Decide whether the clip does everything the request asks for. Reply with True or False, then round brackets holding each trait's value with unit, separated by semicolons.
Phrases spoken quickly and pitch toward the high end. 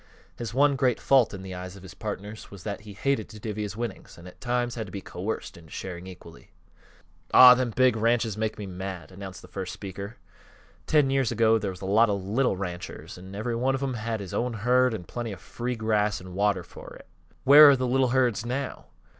False (230 wpm; 110 Hz)